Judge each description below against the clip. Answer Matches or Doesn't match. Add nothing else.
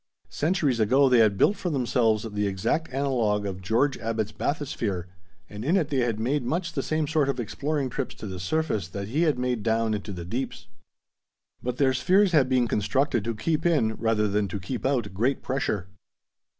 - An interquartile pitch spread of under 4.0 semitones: Doesn't match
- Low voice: Matches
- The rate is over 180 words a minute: Matches